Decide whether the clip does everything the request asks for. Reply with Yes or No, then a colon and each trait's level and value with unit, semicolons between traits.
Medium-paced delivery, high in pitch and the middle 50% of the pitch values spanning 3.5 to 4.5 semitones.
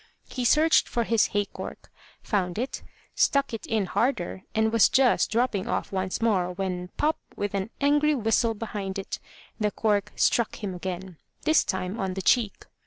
Yes: average, 175 wpm; high, 210 Hz; average, 3.9 semitones